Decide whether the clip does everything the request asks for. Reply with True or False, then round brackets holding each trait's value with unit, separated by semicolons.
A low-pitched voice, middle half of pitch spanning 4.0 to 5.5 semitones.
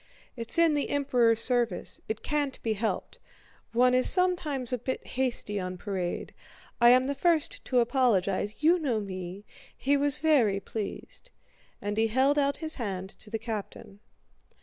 False (245 Hz; 5.2 semitones)